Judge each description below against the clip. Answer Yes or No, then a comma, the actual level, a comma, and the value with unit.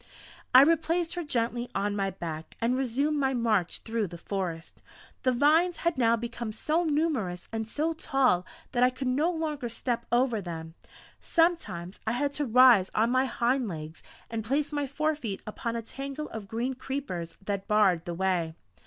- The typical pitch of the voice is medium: No, high, 240 Hz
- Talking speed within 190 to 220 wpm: No, average, 175 wpm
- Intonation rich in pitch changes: Yes, wide, 6.0 semitones